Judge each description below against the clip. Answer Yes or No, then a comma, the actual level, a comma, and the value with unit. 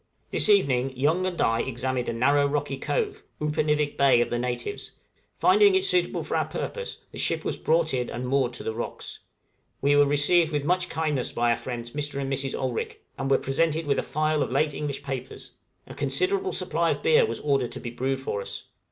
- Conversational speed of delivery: No, fast, 210 wpm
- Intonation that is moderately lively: Yes, average, 3.9 semitones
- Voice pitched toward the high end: No, medium, 145 Hz